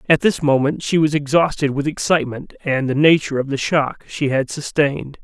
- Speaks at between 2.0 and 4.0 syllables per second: No, 5.4 syllables/s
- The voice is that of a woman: No, male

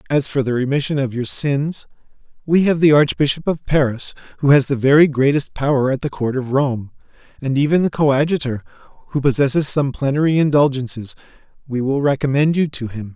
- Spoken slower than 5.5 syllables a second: No, 5.7 syllables/s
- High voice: No, medium, 140 Hz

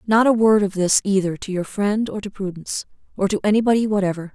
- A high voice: Yes, high, 200 Hz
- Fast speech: Yes, fast, 220 wpm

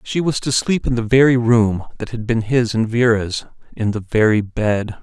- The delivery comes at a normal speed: No, fast, 215 wpm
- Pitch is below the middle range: Yes, low, 115 Hz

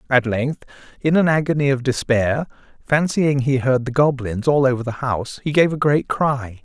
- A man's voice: Yes, male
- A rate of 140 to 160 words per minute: No, average, 190 wpm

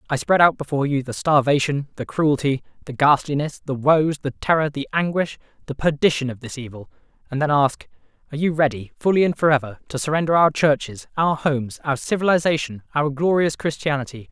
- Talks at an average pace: Yes, average, 175 wpm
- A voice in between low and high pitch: Yes, medium, 145 Hz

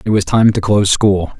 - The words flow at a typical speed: No, fast, 260 wpm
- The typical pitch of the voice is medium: No, low, 100 Hz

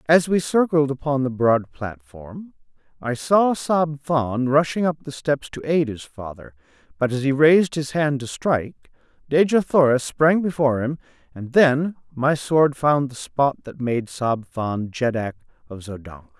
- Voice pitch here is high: No, medium, 140 Hz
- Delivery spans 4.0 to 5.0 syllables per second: Yes, 4.4 syllables/s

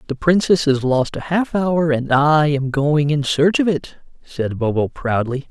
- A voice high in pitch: No, medium, 150 Hz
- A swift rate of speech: No, average, 195 wpm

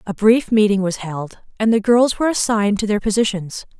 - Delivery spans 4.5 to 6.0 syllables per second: Yes, 5.5 syllables/s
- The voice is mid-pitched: No, high, 210 Hz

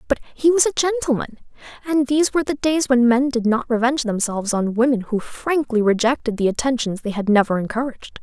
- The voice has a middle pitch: No, very high, 250 Hz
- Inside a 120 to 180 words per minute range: No, average, 195 wpm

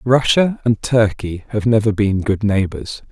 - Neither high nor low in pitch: No, low, 110 Hz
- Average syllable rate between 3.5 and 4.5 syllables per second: Yes, 4.2 syllables/s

